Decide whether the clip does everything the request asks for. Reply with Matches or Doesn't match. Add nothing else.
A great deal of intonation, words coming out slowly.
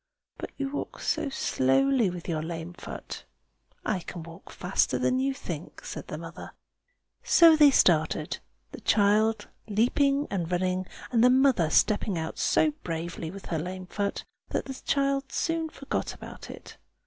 Doesn't match